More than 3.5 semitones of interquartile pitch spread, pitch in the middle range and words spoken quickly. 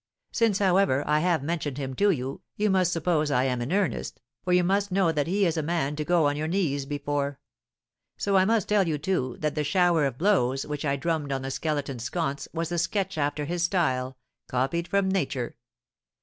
Yes: average, 4.4 semitones; medium, 160 Hz; fast, 210 wpm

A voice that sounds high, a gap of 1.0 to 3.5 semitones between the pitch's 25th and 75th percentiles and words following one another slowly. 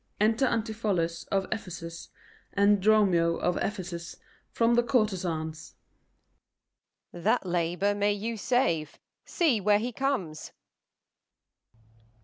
No: high, 200 Hz; average, 4.4 semitones; slow, 105 wpm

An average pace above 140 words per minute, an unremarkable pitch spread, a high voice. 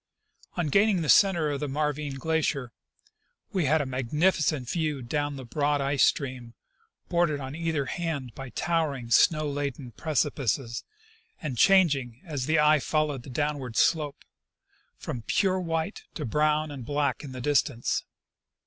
No: average, 155 wpm; average, 3.1 semitones; medium, 145 Hz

